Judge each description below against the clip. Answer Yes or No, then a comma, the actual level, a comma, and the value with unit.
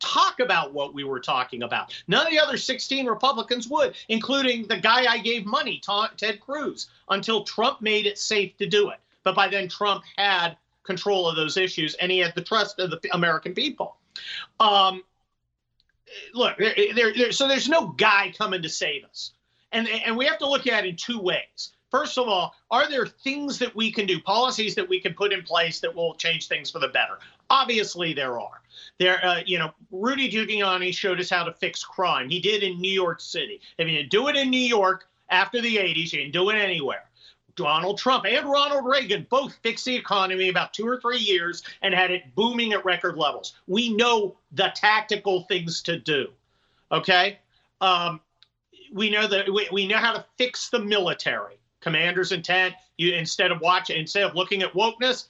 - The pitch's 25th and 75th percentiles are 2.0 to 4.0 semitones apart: No, average, 4.5 semitones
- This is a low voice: No, high, 200 Hz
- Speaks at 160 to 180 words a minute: No, average, 200 wpm